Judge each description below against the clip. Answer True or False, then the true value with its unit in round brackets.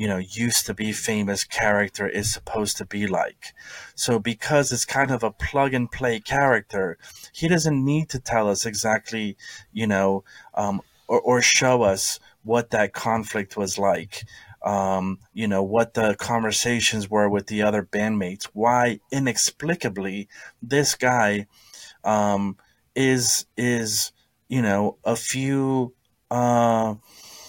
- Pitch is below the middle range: True (110 Hz)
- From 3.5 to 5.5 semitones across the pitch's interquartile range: False (3.0 semitones)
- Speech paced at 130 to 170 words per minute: True (135 wpm)